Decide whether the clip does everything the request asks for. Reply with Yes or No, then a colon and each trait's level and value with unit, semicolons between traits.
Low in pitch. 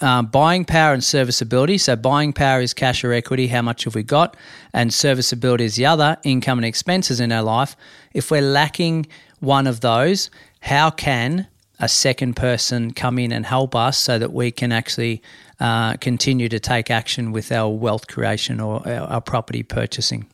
Yes: low, 125 Hz